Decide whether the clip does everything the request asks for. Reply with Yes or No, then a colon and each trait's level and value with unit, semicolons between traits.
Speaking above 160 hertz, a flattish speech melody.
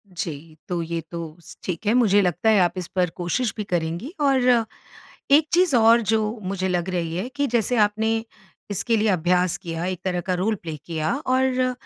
No: high, 190 Hz; average, 4.7 semitones